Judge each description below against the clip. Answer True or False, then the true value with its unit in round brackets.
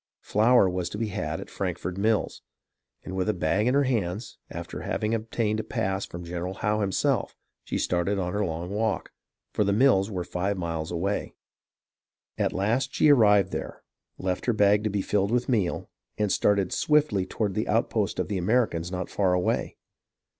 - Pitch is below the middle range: True (100 Hz)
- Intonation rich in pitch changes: False (3.0 semitones)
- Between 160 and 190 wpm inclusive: True (180 wpm)